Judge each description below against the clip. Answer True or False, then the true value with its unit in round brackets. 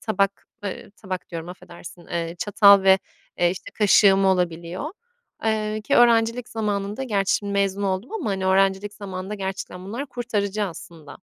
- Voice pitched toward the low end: False (195 Hz)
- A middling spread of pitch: False (2.2 semitones)